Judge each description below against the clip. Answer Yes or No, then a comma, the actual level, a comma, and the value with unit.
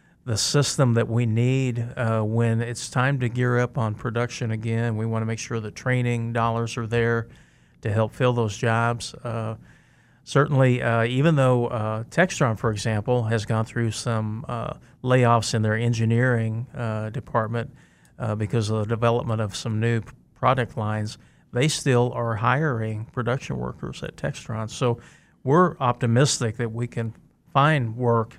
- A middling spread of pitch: No, narrow, 2.0 semitones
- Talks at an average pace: Yes, average, 160 wpm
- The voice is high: No, low, 120 Hz